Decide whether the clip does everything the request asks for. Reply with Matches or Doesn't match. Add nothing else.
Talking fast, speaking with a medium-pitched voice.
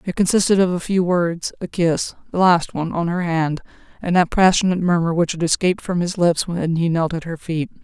Matches